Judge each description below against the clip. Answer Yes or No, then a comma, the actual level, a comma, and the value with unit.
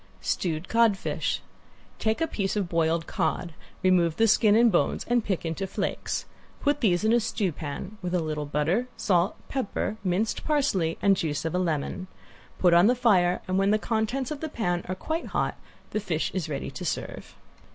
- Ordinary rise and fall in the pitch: Yes, average, 4.6 semitones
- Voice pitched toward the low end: No, high, 190 Hz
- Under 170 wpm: No, average, 185 wpm